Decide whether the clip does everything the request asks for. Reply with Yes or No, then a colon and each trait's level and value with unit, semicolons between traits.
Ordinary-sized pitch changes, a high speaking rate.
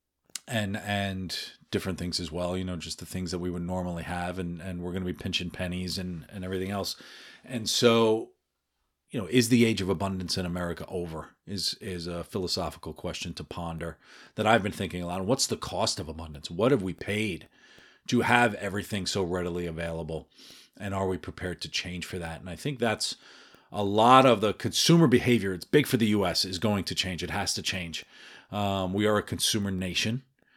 Yes: average, 3.1 semitones; fast, 210 wpm